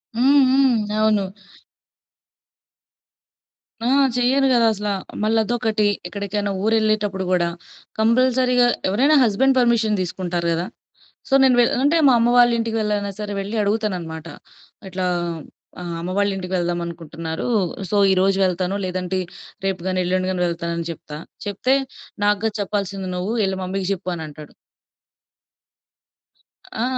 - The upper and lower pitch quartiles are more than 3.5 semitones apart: Yes, average, 3.9 semitones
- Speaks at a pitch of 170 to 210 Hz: Yes, high, 200 Hz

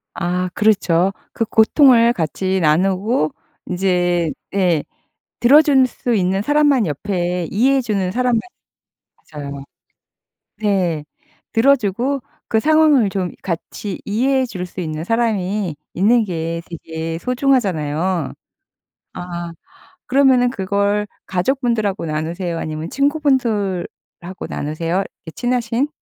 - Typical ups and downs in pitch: No, wide, 5.9 semitones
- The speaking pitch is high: Yes, high, 195 Hz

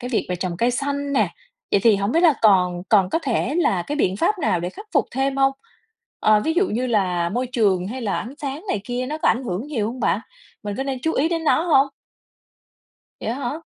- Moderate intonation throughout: No, wide, 5.9 semitones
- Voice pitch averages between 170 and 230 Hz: No, high, 245 Hz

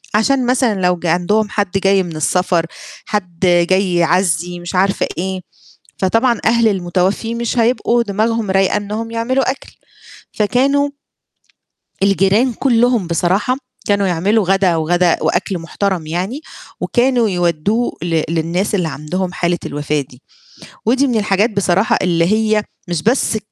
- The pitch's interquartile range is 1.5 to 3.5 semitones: No, average, 4.4 semitones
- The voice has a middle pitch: No, high, 195 Hz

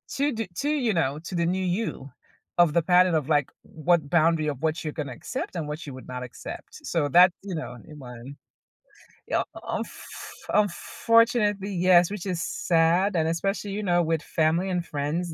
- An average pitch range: Yes, average, 3.7 semitones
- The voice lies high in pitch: No, medium, 170 Hz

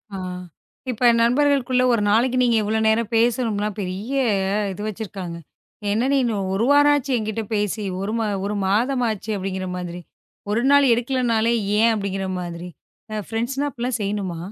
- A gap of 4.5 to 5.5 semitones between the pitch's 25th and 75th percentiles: No, average, 3.6 semitones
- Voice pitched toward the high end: Yes, high, 225 Hz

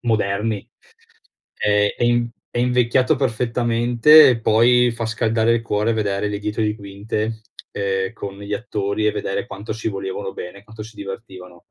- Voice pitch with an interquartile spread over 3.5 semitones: No, narrow, 2.6 semitones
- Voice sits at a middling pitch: No, low, 110 Hz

